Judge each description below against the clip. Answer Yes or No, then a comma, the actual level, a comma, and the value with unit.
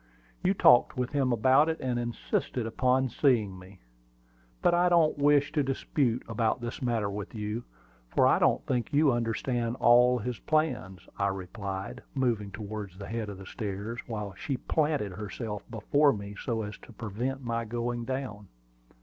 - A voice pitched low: Yes, low, 120 Hz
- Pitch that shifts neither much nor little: Yes, average, 4.1 semitones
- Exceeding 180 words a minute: No, average, 165 wpm